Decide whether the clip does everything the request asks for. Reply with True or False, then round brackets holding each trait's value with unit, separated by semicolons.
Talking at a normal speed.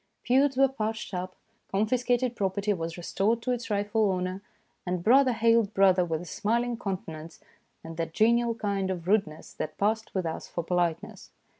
True (165 wpm)